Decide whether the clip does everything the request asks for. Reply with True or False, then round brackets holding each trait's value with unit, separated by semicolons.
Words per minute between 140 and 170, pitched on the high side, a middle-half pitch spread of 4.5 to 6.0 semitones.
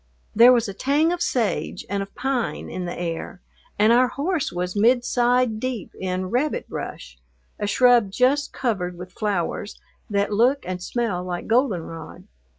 True (155 wpm; 220 Hz; 5.4 semitones)